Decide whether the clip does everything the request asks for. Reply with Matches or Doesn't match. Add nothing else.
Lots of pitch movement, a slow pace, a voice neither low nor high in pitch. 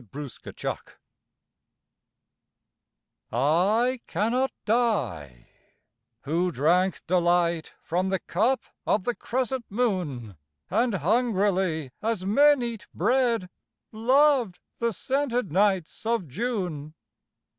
Doesn't match